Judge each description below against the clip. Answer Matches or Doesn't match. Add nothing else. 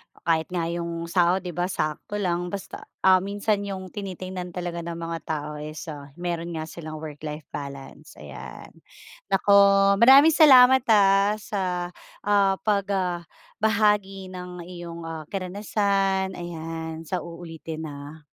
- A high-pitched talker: Doesn't match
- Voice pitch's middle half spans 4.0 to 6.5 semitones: Doesn't match